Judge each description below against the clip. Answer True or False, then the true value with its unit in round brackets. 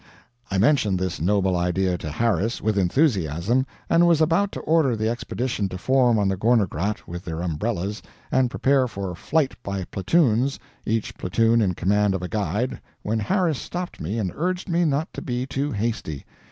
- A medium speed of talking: True (180 wpm)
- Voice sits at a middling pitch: False (110 Hz)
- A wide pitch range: True (6.0 semitones)